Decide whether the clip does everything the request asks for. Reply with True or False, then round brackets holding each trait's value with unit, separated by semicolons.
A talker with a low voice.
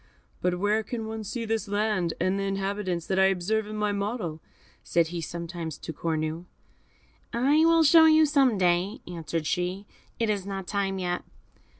False (195 Hz)